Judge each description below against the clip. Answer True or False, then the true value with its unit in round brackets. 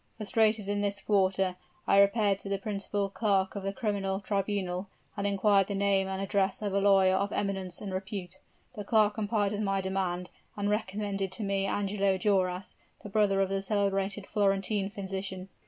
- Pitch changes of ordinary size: False (1.1 semitones)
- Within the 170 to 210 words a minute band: True (175 wpm)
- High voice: True (195 Hz)